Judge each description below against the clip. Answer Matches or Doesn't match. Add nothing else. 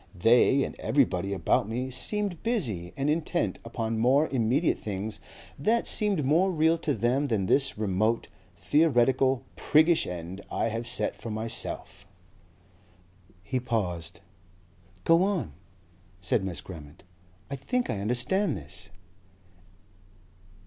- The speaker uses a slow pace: Matches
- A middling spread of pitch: Doesn't match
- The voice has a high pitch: Doesn't match